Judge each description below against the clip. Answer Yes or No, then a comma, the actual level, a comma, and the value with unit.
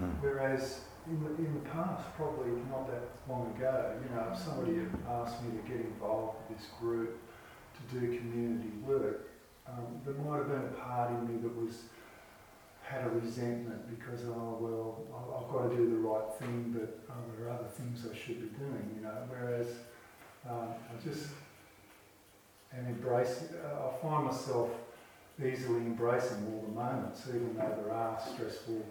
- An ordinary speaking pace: Yes, average, 175 wpm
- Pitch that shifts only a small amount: Yes, narrow, 2.2 semitones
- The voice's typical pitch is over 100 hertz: Yes, low, 120 Hz